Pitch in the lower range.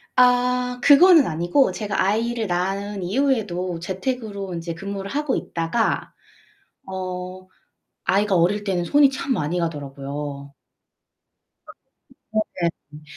No: high, 195 Hz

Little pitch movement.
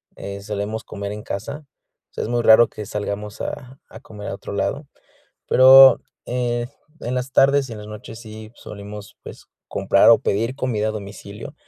No: average, 3.5 semitones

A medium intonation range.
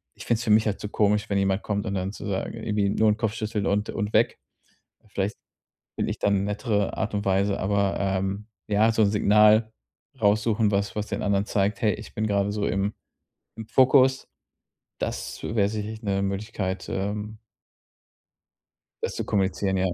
No: narrow, 1.5 semitones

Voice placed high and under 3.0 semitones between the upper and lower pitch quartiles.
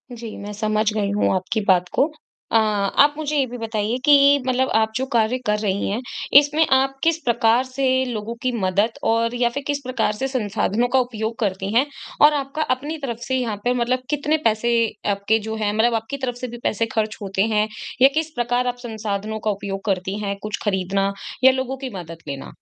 No: high, 230 Hz; average, 3.7 semitones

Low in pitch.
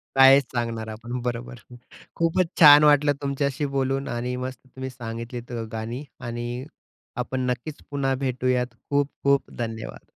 Yes: low, 130 Hz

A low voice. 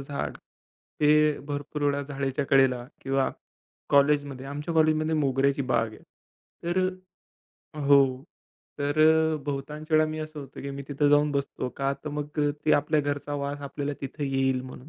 No: medium, 145 Hz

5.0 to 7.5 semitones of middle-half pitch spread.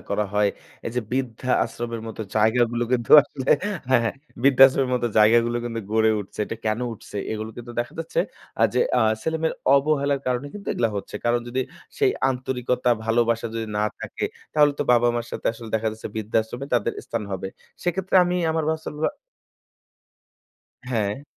No: average, 3.1 semitones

